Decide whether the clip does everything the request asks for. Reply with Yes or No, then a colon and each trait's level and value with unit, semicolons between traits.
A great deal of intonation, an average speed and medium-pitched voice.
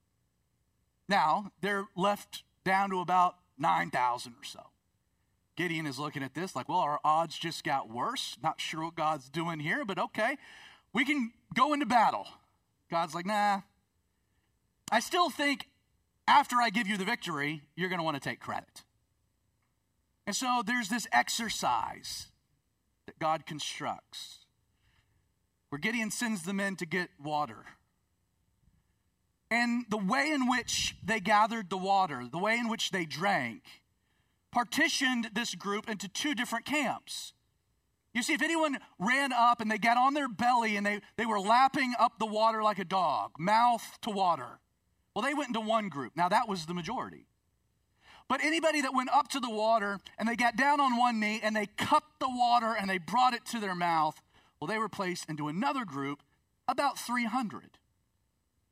No: wide, 7.4 semitones; average, 170 wpm; high, 205 Hz